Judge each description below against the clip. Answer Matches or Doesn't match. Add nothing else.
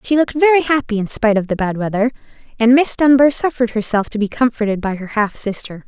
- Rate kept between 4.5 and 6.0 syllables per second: Doesn't match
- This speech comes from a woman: Matches